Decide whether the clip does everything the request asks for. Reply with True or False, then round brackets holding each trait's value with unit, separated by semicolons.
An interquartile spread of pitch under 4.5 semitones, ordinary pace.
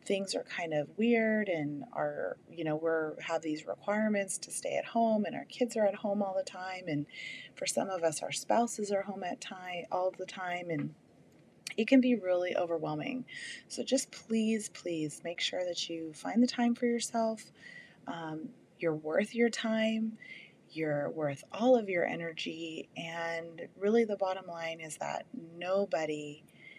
False (5.2 semitones; 175 wpm)